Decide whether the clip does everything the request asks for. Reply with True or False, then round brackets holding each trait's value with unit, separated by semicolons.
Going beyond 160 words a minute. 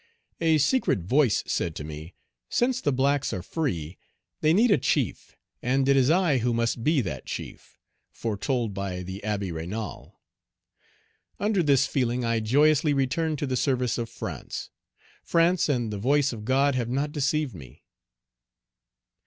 False (155 wpm)